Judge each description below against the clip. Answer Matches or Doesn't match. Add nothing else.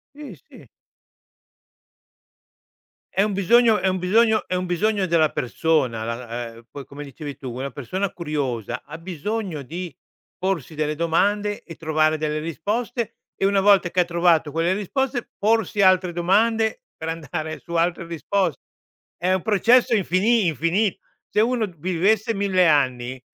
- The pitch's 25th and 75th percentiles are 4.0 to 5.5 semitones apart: Matches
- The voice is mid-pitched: Matches